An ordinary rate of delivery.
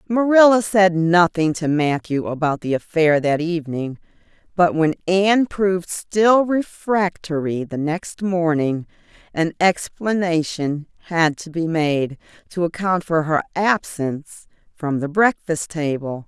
No: slow, 125 wpm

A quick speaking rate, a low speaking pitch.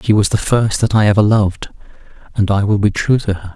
Yes: fast, 255 wpm; low, 105 Hz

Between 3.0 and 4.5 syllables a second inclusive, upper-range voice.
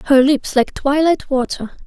Yes: 4.0 syllables/s; very high, 275 Hz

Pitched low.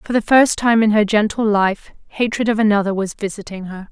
No: high, 210 Hz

